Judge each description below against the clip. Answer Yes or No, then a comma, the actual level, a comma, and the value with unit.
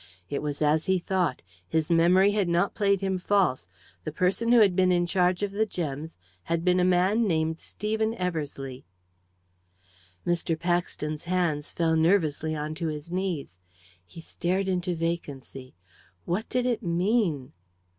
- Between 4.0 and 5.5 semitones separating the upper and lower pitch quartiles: No, average, 3.3 semitones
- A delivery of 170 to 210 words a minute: No, average, 155 wpm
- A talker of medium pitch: Yes, medium, 175 Hz